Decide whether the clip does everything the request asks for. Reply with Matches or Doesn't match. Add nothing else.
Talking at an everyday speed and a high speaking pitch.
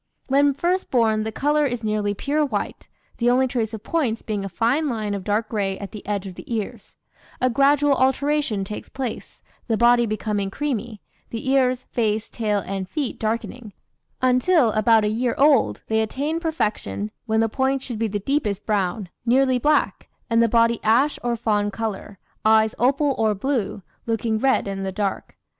Matches